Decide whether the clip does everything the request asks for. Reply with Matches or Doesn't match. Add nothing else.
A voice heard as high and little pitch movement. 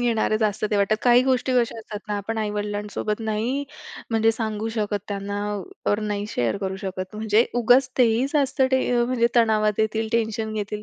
Matches